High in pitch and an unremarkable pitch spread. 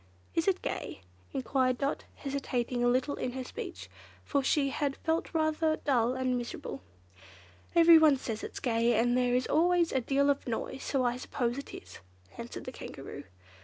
Yes: very high, 265 Hz; average, 3.3 semitones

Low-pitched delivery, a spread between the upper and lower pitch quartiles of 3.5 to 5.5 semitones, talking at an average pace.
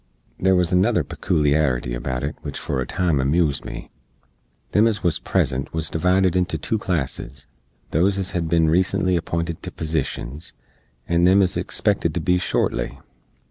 Yes: very low, 85 Hz; average, 4.1 semitones; average, 160 wpm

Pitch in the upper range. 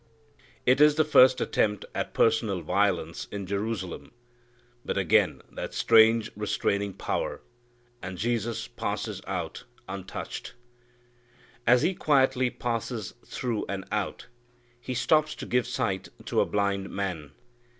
No: low, 110 Hz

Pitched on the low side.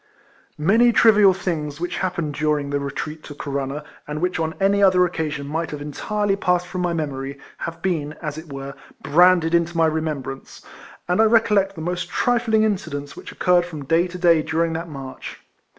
No: medium, 165 Hz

